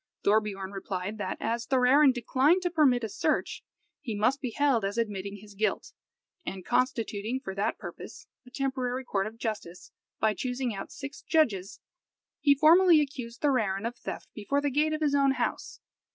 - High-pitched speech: Yes, high, 245 Hz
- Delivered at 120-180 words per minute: Yes, average, 170 wpm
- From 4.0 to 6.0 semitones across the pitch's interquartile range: Yes, average, 5.0 semitones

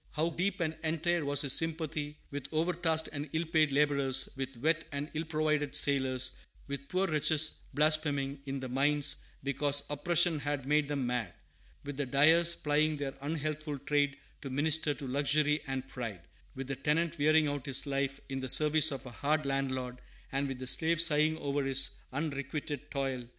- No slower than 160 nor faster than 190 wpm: Yes, average, 170 wpm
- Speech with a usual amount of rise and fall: No, narrow, 2.3 semitones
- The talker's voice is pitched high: No, medium, 145 Hz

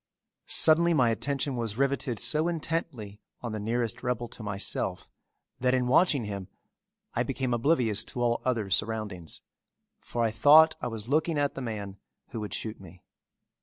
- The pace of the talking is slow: No, average, 165 wpm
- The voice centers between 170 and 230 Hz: No, low, 120 Hz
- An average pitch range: Yes, average, 4.4 semitones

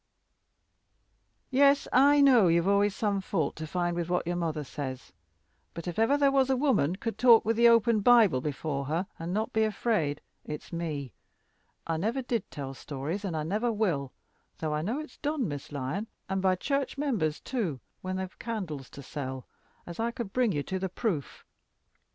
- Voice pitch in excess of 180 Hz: Yes, high, 190 Hz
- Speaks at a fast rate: No, average, 190 wpm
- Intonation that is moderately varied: No, wide, 7.1 semitones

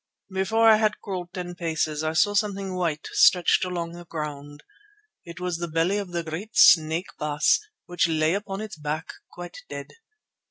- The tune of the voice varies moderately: Yes, average, 3.4 semitones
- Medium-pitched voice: Yes, medium, 175 Hz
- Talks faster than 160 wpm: Yes, average, 170 wpm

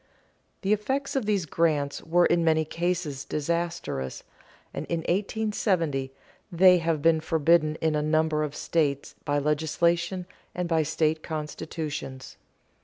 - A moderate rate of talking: No, slow, 130 wpm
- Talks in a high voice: No, medium, 160 Hz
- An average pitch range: No, narrow, 2.3 semitones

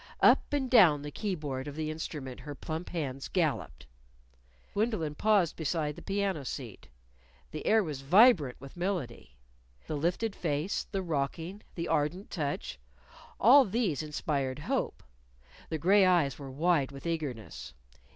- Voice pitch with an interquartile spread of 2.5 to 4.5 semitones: No, average, 5.2 semitones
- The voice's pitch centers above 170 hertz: No, medium, 155 Hz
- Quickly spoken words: No, average, 145 wpm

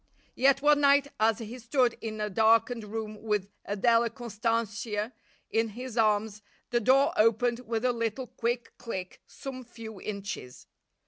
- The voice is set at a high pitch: Yes, high, 230 Hz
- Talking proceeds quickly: No, average, 145 wpm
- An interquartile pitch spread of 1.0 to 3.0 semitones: Yes, narrow, 2.4 semitones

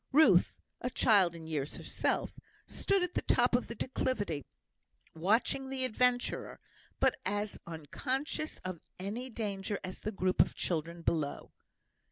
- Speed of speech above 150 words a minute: No, average, 140 wpm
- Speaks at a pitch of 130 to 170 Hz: No, high, 205 Hz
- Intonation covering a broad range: Yes, wide, 7.1 semitones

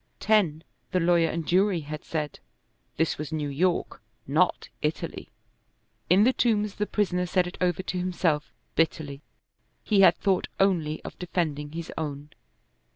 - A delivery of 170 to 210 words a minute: No, average, 150 wpm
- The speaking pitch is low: No, medium, 170 Hz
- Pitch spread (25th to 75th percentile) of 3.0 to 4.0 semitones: Yes, average, 3.4 semitones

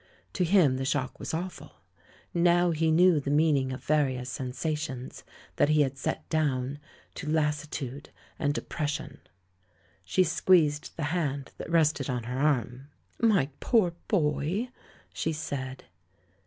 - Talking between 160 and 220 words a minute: No, slow, 135 wpm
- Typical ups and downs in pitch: Yes, average, 3.4 semitones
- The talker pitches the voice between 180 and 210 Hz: No, medium, 150 Hz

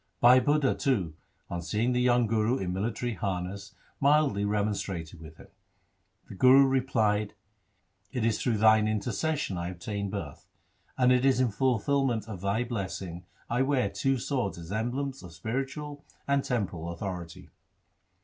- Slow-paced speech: No, average, 150 wpm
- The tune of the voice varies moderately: Yes, average, 4.7 semitones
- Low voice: Yes, low, 110 Hz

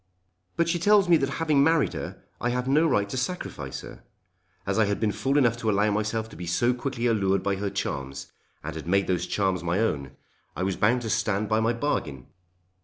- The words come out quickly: Yes, fast, 220 wpm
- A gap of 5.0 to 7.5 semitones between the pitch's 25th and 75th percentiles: Yes, wide, 5.4 semitones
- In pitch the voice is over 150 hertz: No, low, 110 Hz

